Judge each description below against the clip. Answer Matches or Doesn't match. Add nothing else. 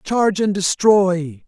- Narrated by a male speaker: Matches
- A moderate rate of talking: Doesn't match